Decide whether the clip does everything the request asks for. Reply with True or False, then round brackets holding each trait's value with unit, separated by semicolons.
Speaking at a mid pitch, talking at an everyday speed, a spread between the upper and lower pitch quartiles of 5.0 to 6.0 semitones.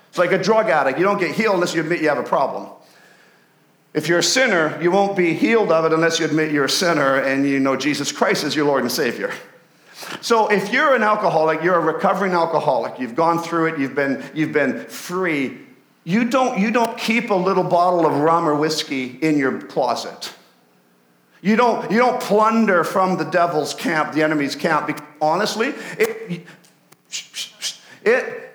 True (170 Hz; 190 wpm; 5.6 semitones)